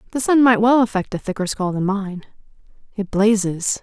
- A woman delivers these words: Yes, female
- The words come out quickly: No, average, 190 wpm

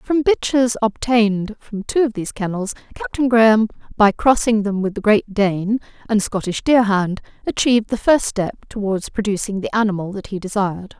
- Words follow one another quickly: No, average, 170 wpm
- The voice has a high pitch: Yes, high, 215 Hz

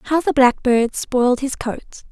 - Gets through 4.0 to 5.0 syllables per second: Yes, 4.4 syllables/s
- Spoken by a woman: Yes, female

